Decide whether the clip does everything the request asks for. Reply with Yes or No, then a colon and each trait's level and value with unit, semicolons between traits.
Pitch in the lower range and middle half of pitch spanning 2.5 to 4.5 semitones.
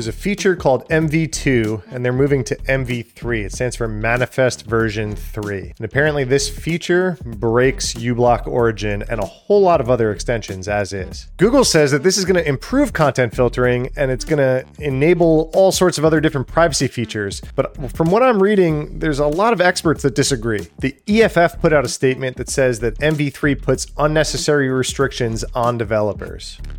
No: low, 130 Hz; average, 5.3 semitones